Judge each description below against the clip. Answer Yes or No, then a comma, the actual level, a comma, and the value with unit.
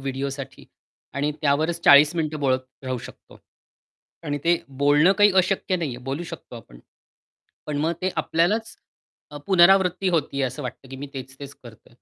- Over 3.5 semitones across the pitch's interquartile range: Yes, average, 4.2 semitones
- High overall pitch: No, medium, 145 Hz